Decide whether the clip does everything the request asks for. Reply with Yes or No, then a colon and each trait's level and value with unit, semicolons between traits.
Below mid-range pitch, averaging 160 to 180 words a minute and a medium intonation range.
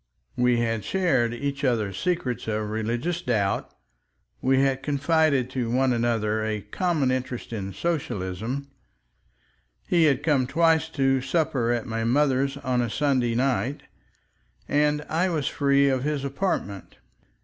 No: low, 130 Hz; average, 140 wpm; average, 3.9 semitones